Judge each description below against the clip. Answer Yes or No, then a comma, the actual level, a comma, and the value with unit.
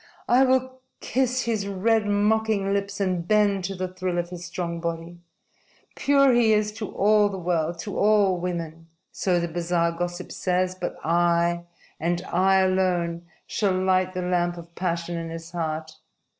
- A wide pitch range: No, average, 2.9 semitones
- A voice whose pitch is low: No, medium, 185 Hz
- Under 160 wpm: No, average, 165 wpm